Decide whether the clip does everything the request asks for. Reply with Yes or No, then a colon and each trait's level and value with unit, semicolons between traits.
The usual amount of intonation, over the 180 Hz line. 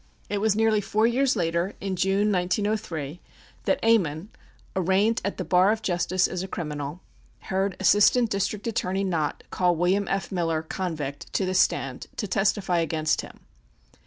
Yes: average, 3.2 semitones; high, 190 Hz